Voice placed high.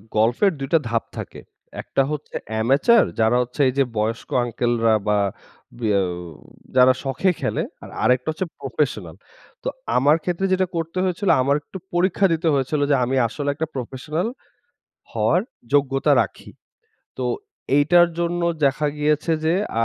No: medium, 140 Hz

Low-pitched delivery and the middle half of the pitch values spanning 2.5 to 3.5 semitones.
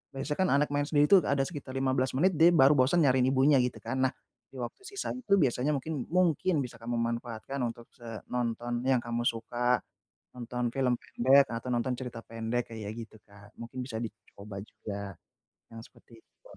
Yes: low, 125 Hz; average, 3.2 semitones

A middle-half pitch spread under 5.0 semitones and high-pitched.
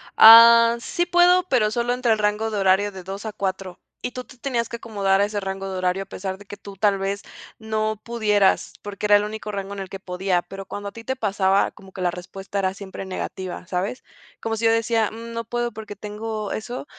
Yes: average, 2.8 semitones; high, 205 Hz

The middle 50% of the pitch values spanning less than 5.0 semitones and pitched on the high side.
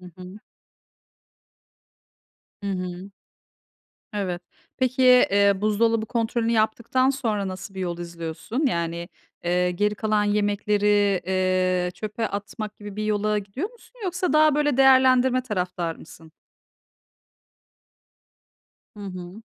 Yes: average, 4.3 semitones; high, 205 Hz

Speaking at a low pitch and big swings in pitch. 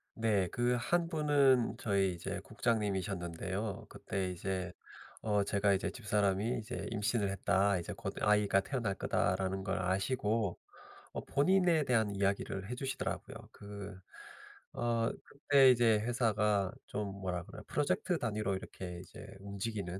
No: low, 105 Hz; average, 3.5 semitones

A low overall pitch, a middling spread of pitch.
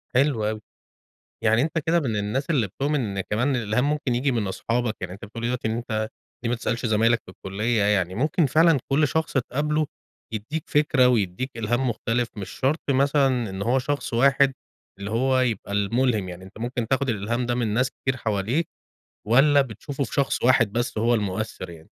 Yes: low, 120 Hz; average, 3.9 semitones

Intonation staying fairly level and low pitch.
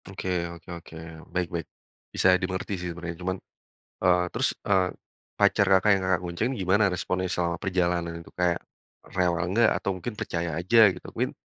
Yes: narrow, 1.5 semitones; very low, 90 Hz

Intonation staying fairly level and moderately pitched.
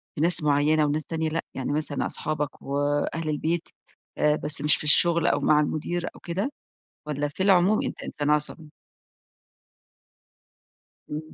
Yes: narrow, 2.0 semitones; medium, 150 Hz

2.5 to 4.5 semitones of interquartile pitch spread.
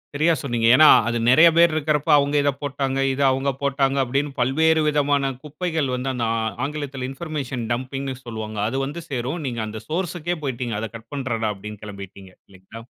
Yes: average, 3.9 semitones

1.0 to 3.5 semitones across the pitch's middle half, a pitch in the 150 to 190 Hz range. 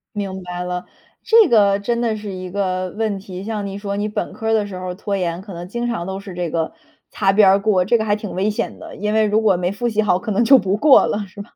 No: narrow, 2.6 semitones; high, 200 Hz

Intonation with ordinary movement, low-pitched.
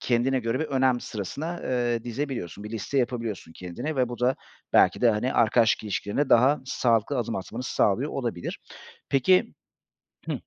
Yes: average, 3.0 semitones; low, 120 Hz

